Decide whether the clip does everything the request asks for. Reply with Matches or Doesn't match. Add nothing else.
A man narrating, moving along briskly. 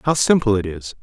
Matches